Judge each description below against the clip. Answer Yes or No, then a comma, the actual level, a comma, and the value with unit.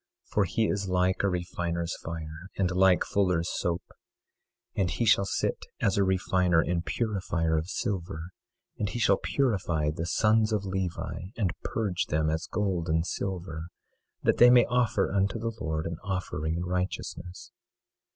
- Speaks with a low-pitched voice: Yes, very low, 90 Hz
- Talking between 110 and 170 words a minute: Yes, average, 160 wpm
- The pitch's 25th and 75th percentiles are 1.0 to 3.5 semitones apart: Yes, average, 3.1 semitones